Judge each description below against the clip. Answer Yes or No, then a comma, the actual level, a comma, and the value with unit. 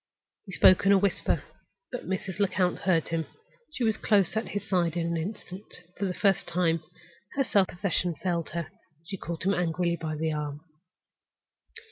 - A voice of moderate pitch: Yes, medium, 180 Hz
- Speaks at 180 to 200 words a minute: Yes, average, 185 wpm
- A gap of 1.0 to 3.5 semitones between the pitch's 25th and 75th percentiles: Yes, average, 3.0 semitones